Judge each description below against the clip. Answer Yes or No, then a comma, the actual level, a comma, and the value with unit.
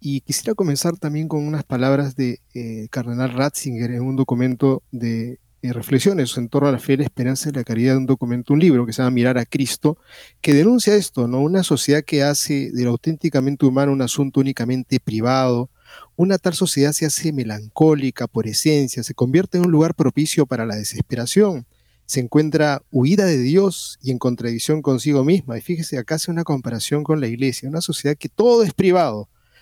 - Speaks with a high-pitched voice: No, medium, 140 Hz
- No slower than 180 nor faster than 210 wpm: Yes, fast, 190 wpm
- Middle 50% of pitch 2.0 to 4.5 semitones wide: Yes, average, 3.7 semitones